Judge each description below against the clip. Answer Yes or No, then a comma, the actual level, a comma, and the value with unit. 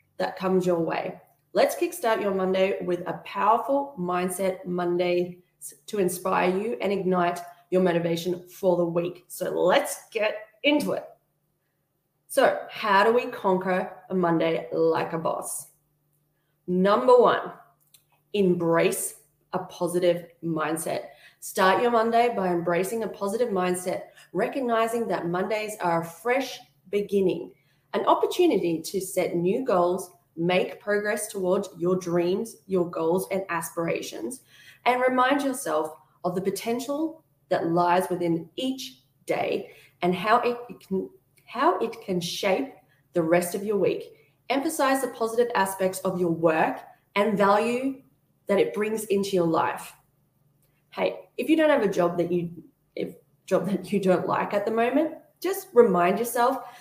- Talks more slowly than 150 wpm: Yes, average, 140 wpm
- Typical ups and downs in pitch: Yes, average, 4.6 semitones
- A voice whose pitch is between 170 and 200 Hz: Yes, medium, 185 Hz